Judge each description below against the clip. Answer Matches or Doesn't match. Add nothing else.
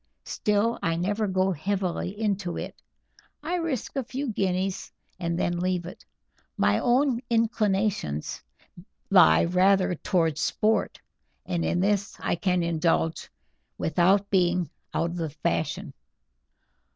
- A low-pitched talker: Doesn't match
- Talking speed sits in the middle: Doesn't match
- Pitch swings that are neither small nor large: Matches